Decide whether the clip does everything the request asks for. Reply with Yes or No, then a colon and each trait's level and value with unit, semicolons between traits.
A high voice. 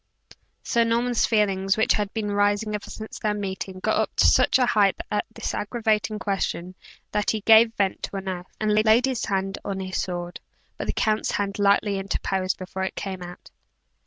Yes: high, 205 Hz